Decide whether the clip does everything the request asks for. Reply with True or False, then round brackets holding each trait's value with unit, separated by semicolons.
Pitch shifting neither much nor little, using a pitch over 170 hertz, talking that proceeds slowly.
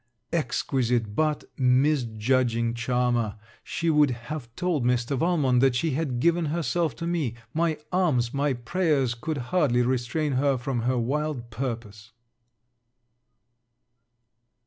False (4.3 semitones; 130 Hz; 125 wpm)